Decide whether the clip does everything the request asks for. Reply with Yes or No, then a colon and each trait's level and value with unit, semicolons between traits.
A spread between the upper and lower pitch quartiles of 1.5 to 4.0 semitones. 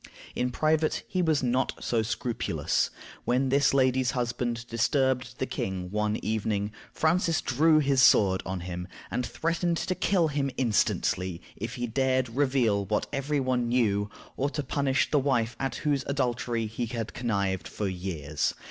No: average, 4.4 semitones